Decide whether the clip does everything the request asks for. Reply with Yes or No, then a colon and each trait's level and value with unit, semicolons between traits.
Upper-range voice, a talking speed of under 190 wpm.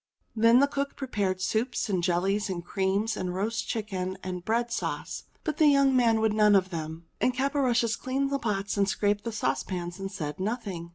No: high, 210 Hz; average, 195 wpm